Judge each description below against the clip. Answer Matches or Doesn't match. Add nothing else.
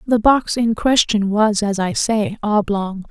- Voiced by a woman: Matches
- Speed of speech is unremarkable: Matches